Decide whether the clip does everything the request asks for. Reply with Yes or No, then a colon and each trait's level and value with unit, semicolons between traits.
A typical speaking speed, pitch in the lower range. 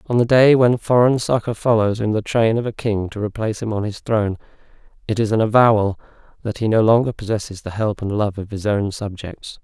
No: fast, 225 wpm; low, 110 Hz